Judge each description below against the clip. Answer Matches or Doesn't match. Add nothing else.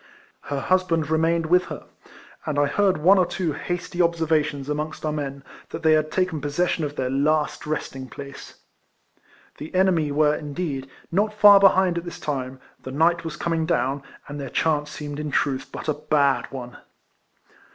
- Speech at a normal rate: Matches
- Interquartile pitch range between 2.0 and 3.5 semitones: Matches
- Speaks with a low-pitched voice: Doesn't match